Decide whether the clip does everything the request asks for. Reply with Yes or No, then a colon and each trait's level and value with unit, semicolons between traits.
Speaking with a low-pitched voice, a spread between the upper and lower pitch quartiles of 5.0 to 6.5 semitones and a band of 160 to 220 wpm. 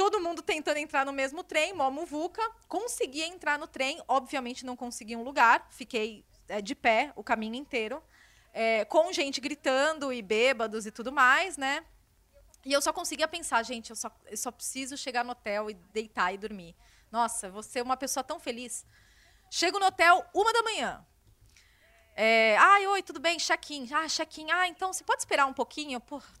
No: very high, 275 Hz; wide, 5.5 semitones; fast, 185 wpm